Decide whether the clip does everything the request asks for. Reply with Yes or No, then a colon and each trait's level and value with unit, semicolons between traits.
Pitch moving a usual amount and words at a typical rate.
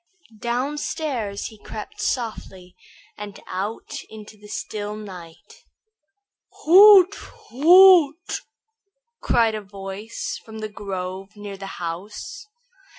No: average, 5.0 semitones; slow, 95 wpm